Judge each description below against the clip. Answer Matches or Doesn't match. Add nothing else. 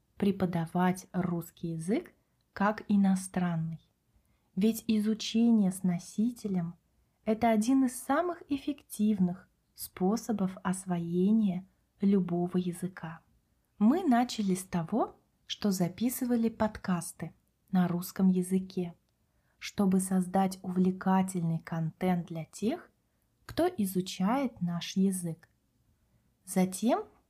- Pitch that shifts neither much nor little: Matches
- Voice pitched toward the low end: Doesn't match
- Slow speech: Matches